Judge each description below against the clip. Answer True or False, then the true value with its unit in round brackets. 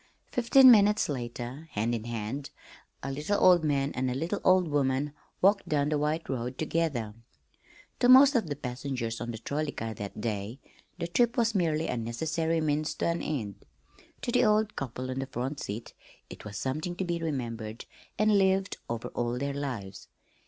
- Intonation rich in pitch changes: True (6.3 semitones)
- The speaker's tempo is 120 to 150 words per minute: False (180 wpm)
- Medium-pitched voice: True (145 Hz)